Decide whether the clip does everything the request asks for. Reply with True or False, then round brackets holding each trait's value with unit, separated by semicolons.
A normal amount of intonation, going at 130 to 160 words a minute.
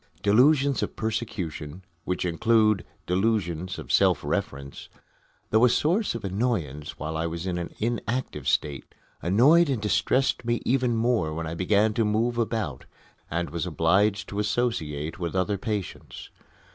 False (5.7 semitones; 145 wpm)